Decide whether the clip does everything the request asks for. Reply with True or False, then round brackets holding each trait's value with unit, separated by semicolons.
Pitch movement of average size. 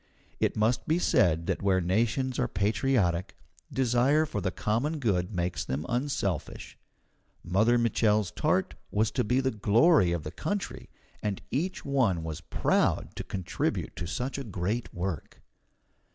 False (6.2 semitones)